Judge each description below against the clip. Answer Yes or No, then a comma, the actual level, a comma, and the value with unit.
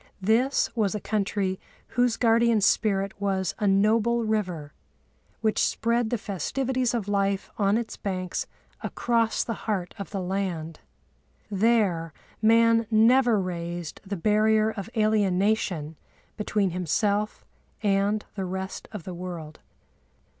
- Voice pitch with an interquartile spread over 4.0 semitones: No, average, 2.9 semitones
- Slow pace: Yes, slow, 125 wpm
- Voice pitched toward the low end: No, high, 205 Hz